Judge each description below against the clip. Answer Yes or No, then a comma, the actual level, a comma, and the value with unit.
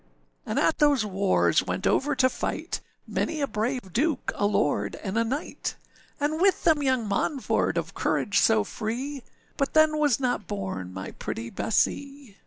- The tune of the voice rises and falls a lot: Yes, wide, 6.0 semitones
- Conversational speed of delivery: Yes, average, 165 wpm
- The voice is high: Yes, very high, 250 Hz